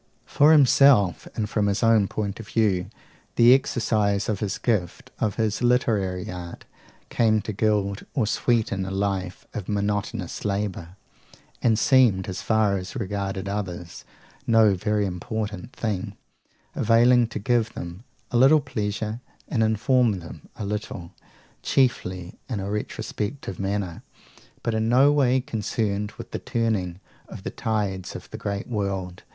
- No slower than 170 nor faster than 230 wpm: No, average, 145 wpm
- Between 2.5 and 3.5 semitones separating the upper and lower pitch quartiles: Yes, average, 3.0 semitones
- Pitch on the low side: Yes, low, 105 Hz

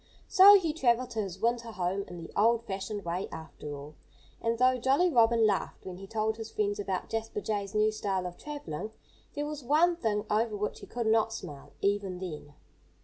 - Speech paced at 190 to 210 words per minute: Yes, average, 200 wpm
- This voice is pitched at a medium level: No, high, 215 Hz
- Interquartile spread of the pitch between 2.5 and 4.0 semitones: Yes, average, 3.6 semitones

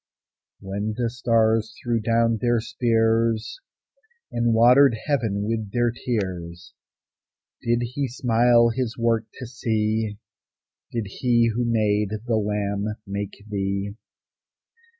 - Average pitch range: No, narrow, 2.2 semitones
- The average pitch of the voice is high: No, low, 115 Hz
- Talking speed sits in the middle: No, slow, 110 wpm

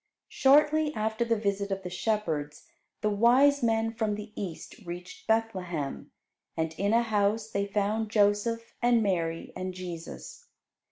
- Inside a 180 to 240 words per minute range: No, average, 145 wpm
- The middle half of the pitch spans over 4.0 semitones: No, average, 3.6 semitones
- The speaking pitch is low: No, high, 210 Hz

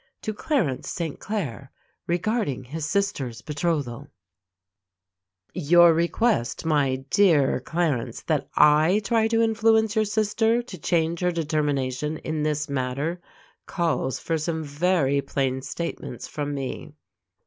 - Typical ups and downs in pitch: Yes, average, 5.0 semitones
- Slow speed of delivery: Yes, slow, 120 wpm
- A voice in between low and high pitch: Yes, medium, 160 Hz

